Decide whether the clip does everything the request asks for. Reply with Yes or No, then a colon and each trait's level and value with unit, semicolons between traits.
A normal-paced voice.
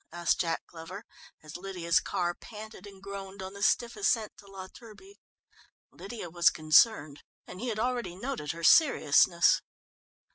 Yes: average, 150 wpm